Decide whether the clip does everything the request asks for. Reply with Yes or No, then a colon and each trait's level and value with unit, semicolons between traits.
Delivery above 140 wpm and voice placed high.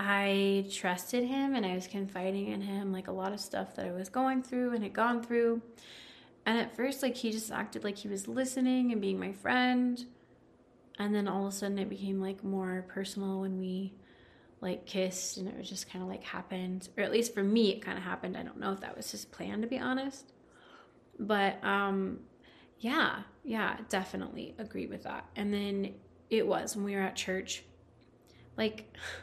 Yes: fast, 205 wpm; high, 200 Hz